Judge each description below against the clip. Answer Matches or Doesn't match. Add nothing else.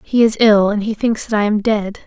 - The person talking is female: Matches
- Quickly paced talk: Matches